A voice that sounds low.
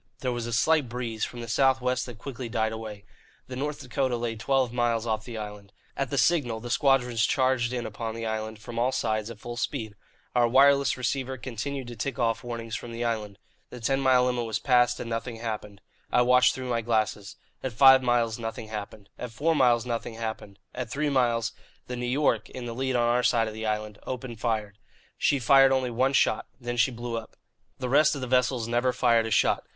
Yes: low, 120 Hz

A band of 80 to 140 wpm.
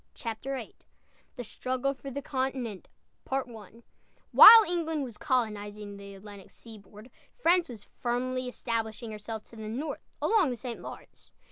Yes: slow, 135 wpm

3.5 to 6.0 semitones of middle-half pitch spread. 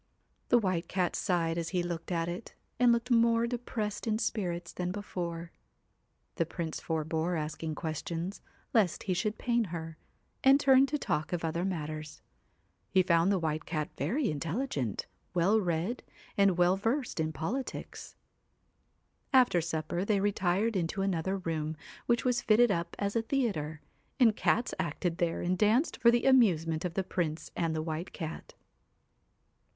Yes: average, 5.2 semitones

